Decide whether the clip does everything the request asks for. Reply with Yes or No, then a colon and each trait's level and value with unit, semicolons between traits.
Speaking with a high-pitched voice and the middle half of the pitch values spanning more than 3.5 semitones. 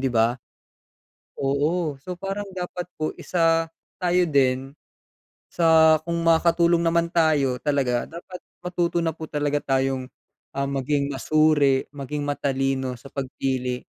No: medium, 150 Hz; average, 3.9 semitones